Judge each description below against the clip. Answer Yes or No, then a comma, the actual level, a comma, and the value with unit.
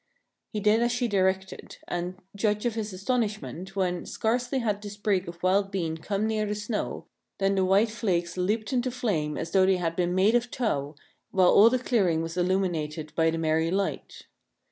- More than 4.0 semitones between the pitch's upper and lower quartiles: No, average, 3.6 semitones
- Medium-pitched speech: No, high, 195 Hz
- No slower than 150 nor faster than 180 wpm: No, average, 190 wpm